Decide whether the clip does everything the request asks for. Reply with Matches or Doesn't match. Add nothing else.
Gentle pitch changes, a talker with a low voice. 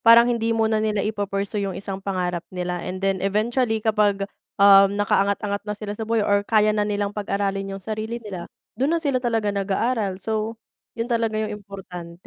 Doesn't match